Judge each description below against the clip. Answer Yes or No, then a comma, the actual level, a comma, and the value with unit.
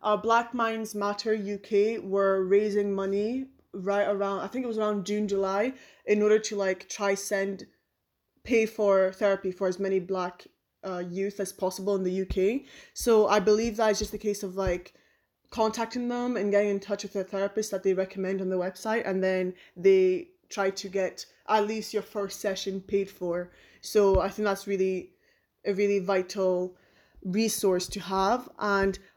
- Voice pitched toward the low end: No, high, 200 Hz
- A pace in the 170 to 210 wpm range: Yes, average, 180 wpm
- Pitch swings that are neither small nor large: No, narrow, 2.0 semitones